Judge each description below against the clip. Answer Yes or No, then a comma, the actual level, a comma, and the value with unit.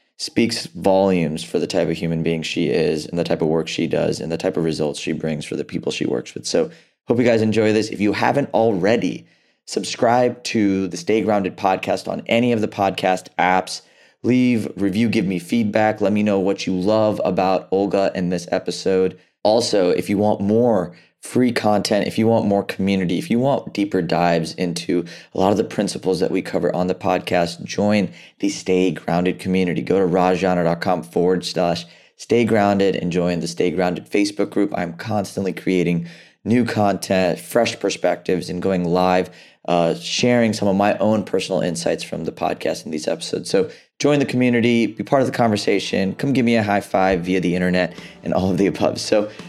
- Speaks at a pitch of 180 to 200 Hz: No, very low, 95 Hz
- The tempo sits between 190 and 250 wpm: Yes, average, 200 wpm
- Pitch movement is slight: No, average, 3.4 semitones